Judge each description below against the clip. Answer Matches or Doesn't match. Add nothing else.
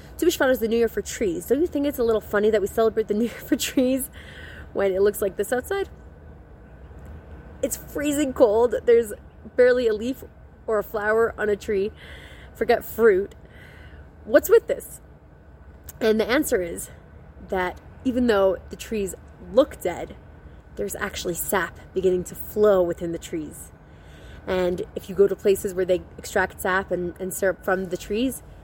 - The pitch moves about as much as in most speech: Doesn't match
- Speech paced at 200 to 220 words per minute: Doesn't match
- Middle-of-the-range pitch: Doesn't match